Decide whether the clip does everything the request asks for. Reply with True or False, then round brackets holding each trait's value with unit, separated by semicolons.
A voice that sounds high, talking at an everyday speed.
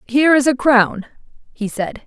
True (250 Hz; 175 wpm)